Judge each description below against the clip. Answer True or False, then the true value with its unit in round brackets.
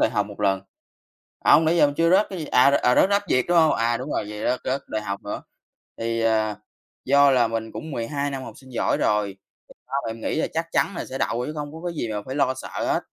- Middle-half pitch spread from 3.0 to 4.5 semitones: False (5.1 semitones)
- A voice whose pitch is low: True (130 Hz)